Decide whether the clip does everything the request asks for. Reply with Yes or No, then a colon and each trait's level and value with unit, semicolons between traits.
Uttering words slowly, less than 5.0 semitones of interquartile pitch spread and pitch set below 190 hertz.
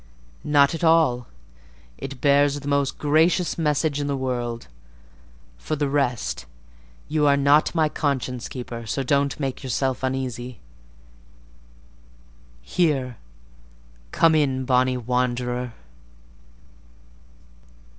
Yes: slow, 100 wpm; average, 2.7 semitones; low, 135 Hz